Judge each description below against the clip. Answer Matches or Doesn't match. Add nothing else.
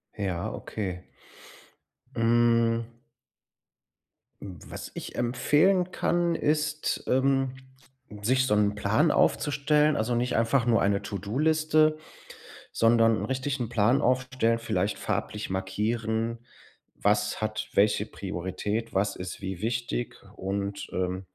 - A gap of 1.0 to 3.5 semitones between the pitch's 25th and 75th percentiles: Doesn't match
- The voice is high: Doesn't match